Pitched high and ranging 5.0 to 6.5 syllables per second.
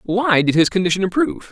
Yes: high, 195 Hz; 6.4 syllables/s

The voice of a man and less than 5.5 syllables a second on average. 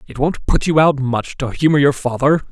Yes: male; 5.1 syllables/s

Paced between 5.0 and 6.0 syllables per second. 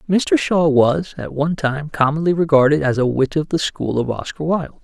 Yes: 5.2 syllables/s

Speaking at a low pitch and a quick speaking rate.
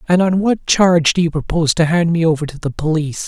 No: medium, 165 Hz; fast, 255 wpm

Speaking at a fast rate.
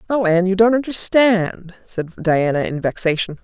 No: average, 155 wpm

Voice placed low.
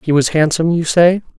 No: medium, 165 Hz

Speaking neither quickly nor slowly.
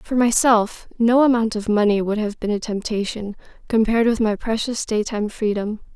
Yes: average, 170 wpm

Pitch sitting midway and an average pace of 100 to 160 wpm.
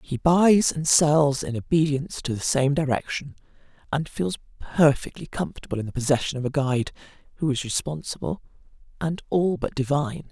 Yes: medium, 150 Hz; average, 155 wpm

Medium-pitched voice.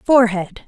No: high, 220 Hz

